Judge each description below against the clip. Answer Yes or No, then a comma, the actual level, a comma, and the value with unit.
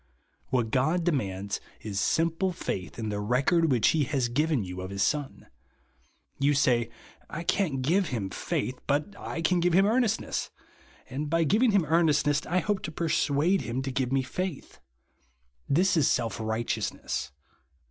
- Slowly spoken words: No, average, 170 wpm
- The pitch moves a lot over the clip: Yes, wide, 6.0 semitones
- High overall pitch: No, medium, 145 Hz